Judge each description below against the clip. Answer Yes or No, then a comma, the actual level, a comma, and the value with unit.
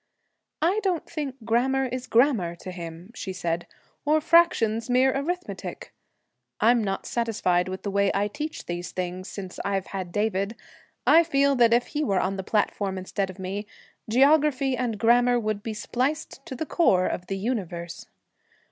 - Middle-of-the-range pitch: No, high, 225 Hz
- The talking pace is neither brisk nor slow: Yes, average, 165 wpm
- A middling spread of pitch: No, wide, 6.0 semitones